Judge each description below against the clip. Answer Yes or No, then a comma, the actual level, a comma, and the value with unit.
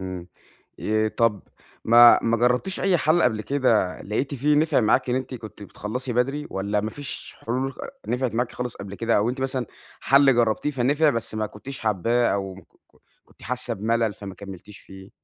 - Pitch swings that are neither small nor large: Yes, average, 3.9 semitones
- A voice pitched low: Yes, low, 115 Hz